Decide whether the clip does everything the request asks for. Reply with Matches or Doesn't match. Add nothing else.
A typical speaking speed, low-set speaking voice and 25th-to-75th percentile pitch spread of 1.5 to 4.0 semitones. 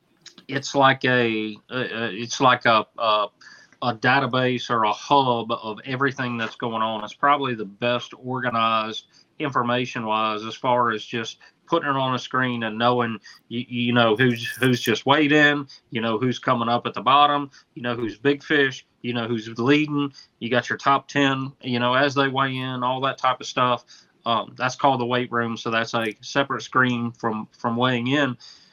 Matches